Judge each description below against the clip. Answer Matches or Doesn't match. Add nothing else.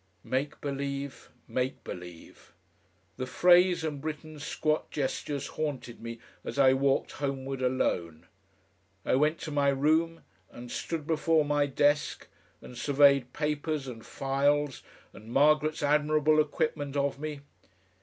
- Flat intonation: Matches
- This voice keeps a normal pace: Doesn't match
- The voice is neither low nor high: Matches